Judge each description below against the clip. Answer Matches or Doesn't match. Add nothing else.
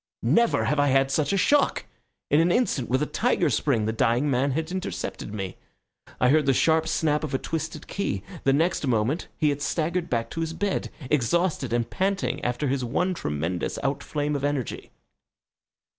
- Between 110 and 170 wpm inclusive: Doesn't match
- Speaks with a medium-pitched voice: Matches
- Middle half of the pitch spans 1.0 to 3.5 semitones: Doesn't match